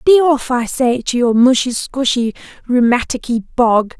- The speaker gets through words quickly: No, average, 150 wpm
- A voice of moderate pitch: No, very high, 250 Hz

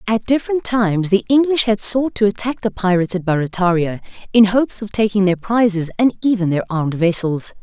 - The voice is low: No, high, 205 Hz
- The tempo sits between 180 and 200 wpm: Yes, average, 190 wpm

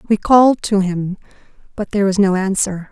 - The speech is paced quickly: No, average, 185 wpm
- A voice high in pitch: Yes, high, 195 Hz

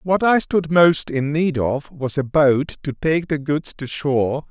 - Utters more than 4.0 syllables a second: No, 3.9 syllables/s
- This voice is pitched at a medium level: Yes, medium, 150 Hz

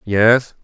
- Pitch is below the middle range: Yes, low, 115 Hz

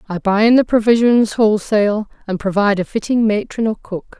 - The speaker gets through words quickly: No, average, 185 wpm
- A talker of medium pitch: No, high, 215 Hz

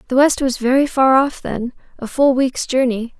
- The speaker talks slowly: No, fast, 205 wpm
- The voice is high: Yes, very high, 260 Hz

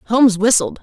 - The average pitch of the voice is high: Yes, high, 225 Hz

